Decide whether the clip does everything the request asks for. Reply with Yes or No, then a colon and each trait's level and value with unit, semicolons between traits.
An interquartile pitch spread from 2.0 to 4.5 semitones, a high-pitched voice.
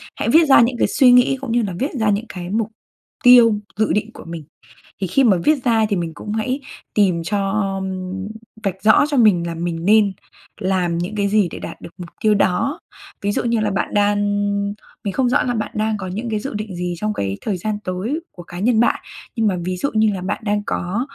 Yes: average, 3.8 semitones; high, 210 Hz